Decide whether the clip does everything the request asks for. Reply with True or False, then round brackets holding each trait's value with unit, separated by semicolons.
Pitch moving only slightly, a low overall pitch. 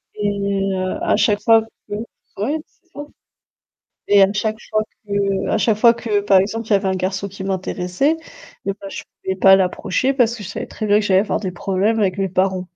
False (2.1 semitones; 200 Hz)